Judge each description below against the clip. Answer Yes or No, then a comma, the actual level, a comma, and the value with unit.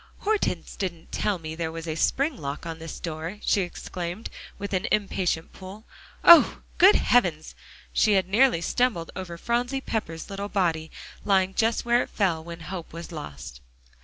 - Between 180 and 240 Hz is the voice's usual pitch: Yes, medium, 185 Hz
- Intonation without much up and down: No, average, 4.7 semitones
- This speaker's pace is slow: No, average, 165 wpm